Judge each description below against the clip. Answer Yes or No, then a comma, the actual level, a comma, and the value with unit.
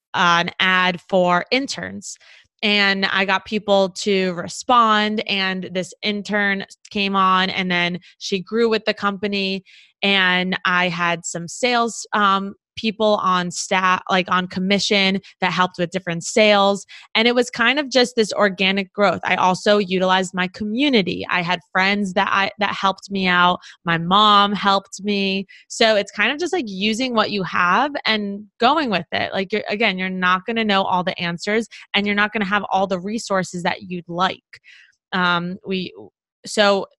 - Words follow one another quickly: No, average, 175 wpm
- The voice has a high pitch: Yes, high, 195 Hz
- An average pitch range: No, narrow, 2.3 semitones